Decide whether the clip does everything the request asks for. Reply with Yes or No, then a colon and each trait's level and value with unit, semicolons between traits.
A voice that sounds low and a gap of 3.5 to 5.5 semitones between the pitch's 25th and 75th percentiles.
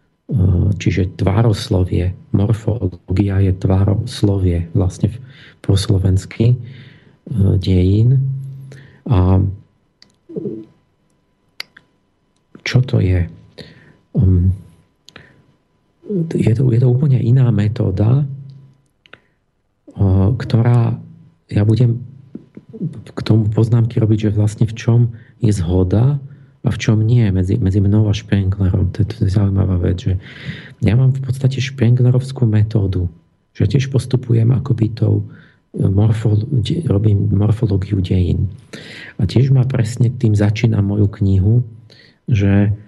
Yes: low, 110 Hz; average, 4.2 semitones